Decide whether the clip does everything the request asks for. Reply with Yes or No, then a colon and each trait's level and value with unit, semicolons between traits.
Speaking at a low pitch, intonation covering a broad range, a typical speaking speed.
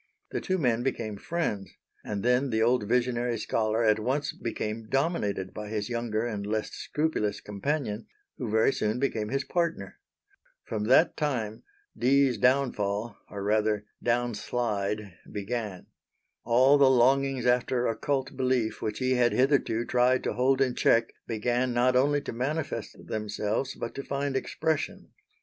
No: low, 120 Hz; average, 3.7 semitones; average, 150 wpm